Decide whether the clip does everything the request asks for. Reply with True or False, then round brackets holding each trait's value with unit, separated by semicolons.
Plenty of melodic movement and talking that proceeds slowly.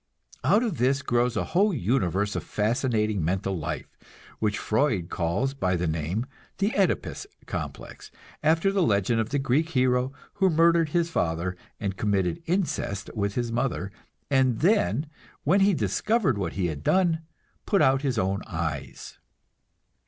False (8.8 semitones; 150 wpm)